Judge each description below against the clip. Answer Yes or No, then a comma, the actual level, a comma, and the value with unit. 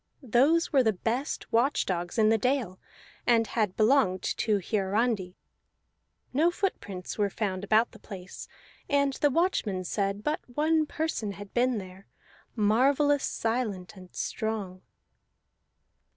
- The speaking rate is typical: No, slow, 130 wpm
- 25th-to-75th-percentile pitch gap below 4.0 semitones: No, wide, 5.6 semitones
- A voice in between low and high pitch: No, high, 220 Hz